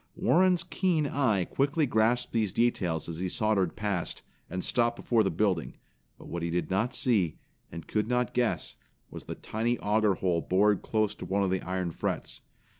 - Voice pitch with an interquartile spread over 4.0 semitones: Yes, average, 4.7 semitones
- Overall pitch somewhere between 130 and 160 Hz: No, low, 105 Hz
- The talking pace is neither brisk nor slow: Yes, average, 185 wpm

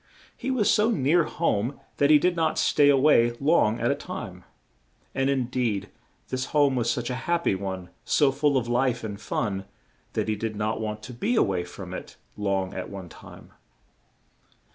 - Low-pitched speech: Yes, low, 125 Hz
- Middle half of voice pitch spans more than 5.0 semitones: Yes, wide, 5.5 semitones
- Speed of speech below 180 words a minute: No, average, 195 wpm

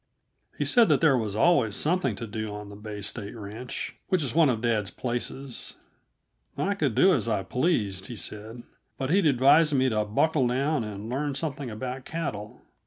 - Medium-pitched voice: No, low, 125 Hz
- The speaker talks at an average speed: Yes, average, 185 wpm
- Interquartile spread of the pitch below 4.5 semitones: No, wide, 5.5 semitones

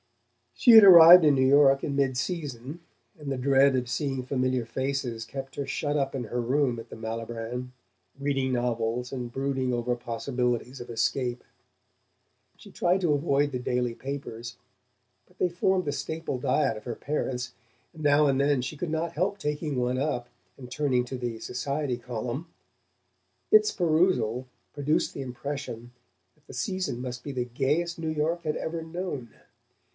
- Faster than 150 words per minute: Yes, average, 165 wpm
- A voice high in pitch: No, low, 135 Hz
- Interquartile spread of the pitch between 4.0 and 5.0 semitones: No, average, 3.5 semitones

